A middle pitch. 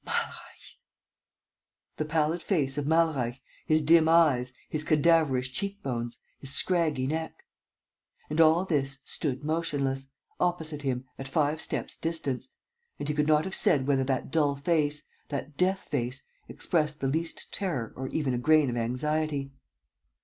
Yes: medium, 150 Hz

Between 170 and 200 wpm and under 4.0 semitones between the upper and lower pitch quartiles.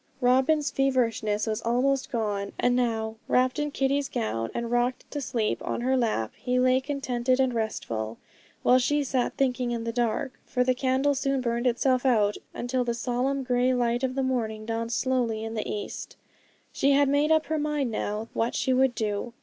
Yes: average, 190 wpm; narrow, 2.5 semitones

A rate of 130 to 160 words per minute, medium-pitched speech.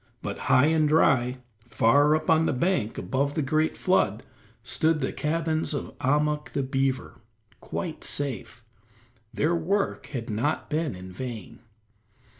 Yes: average, 140 wpm; medium, 145 Hz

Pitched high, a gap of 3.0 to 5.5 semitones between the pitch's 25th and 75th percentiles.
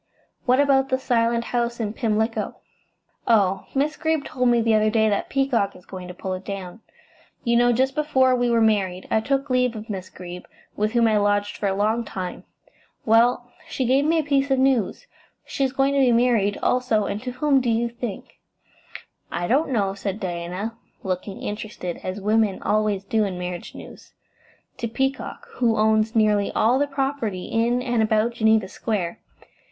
Yes: high, 225 Hz; average, 3.7 semitones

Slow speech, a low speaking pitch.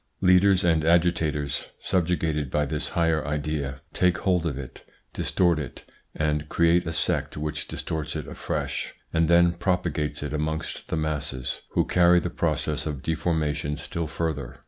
No: average, 150 wpm; very low, 80 Hz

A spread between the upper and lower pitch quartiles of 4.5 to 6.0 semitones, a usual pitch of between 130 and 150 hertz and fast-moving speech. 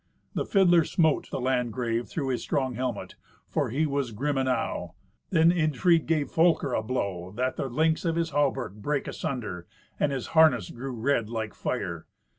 No: average, 5.0 semitones; low, 135 Hz; average, 170 wpm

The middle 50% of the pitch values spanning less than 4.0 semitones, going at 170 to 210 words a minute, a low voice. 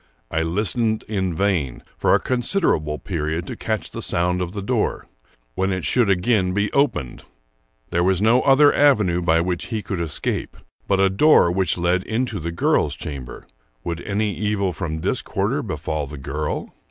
No: average, 4.3 semitones; average, 175 wpm; very low, 95 Hz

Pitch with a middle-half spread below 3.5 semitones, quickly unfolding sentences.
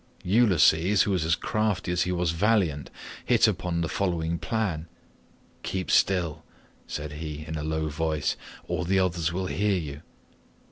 No: average, 3.1 semitones; average, 155 wpm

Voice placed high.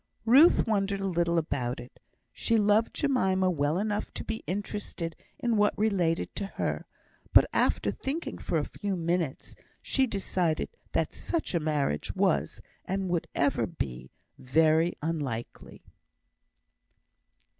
No: medium, 180 Hz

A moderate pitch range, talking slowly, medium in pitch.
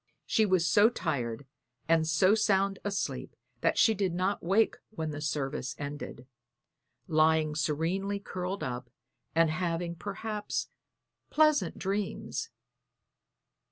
Yes: average, 4.6 semitones; slow, 115 wpm; medium, 175 Hz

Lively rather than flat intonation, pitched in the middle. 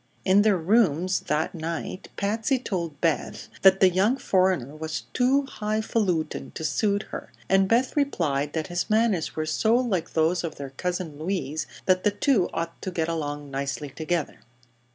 No: average, 4.8 semitones; medium, 180 Hz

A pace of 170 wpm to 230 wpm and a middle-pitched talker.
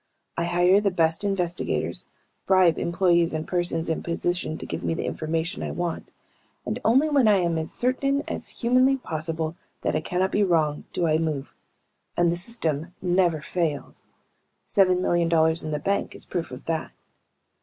Yes: average, 175 wpm; medium, 175 Hz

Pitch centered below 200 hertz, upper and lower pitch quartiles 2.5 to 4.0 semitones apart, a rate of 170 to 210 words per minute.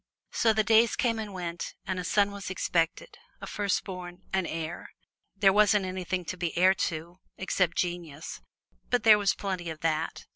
Yes: medium, 185 Hz; average, 2.8 semitones; average, 175 wpm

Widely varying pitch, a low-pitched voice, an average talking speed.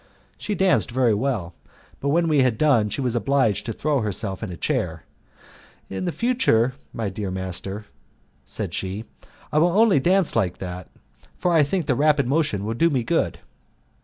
Yes: wide, 7.1 semitones; low, 125 Hz; average, 175 wpm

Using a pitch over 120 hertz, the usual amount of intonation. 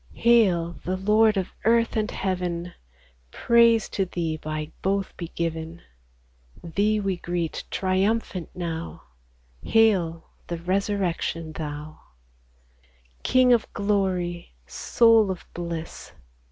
Yes: medium, 185 Hz; average, 3.9 semitones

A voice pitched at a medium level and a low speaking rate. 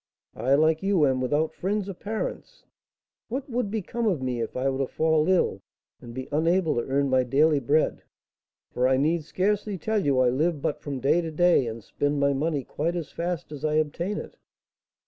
No: medium, 155 Hz; fast, 205 wpm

